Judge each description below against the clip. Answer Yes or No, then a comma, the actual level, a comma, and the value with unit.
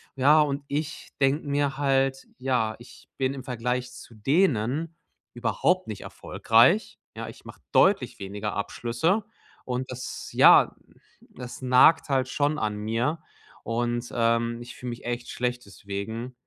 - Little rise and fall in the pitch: No, average, 3.1 semitones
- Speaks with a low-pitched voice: Yes, low, 125 Hz